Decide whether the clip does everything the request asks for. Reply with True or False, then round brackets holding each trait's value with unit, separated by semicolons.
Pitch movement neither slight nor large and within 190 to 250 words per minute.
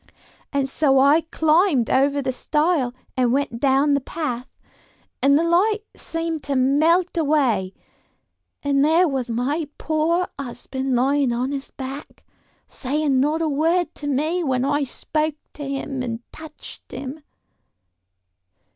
False (3.1 semitones; 140 wpm)